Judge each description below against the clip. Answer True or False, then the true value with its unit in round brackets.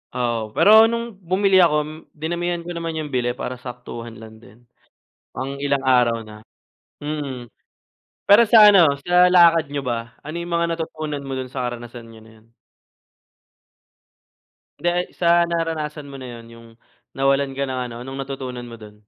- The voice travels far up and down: True (5.7 semitones)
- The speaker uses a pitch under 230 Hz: True (140 Hz)